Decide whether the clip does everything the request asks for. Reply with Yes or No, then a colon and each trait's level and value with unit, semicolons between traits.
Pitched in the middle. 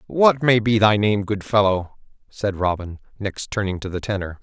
No: low, 100 Hz